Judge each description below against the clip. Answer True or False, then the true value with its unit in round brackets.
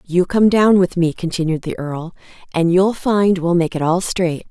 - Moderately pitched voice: True (180 Hz)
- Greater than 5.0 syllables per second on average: False (4.6 syllables/s)